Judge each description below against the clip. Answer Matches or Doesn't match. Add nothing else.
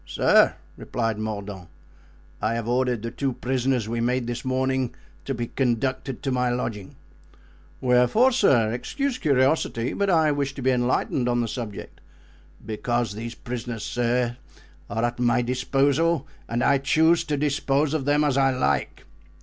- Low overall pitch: Matches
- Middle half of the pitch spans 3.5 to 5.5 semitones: Doesn't match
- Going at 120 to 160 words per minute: Matches